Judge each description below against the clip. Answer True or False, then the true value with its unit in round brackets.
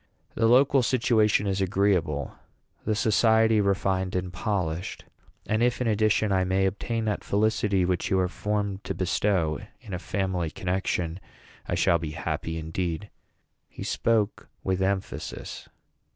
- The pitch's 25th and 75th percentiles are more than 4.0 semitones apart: False (3.0 semitones)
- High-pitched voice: False (95 Hz)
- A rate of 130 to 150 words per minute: True (140 wpm)